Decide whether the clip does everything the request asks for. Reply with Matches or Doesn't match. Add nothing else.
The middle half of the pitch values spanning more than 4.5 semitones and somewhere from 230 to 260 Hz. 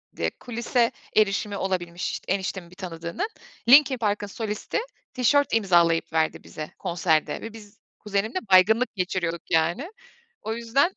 Doesn't match